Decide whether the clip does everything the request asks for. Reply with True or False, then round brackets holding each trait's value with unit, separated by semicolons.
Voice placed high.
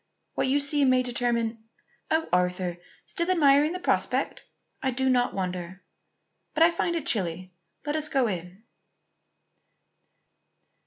True (250 Hz)